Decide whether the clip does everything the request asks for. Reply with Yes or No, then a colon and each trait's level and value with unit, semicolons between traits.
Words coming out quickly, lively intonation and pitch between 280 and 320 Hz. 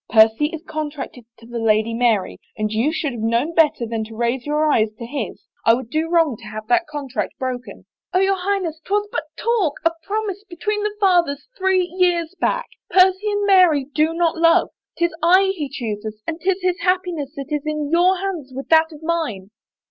Yes: fast, 210 wpm; wide, 6.7 semitones; very high, 315 Hz